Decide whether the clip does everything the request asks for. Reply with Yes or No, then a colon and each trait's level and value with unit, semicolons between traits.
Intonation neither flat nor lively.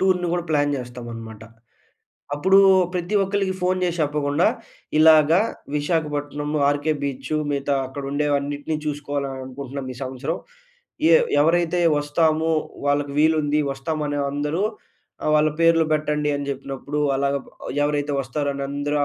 No: narrow, 2.1 semitones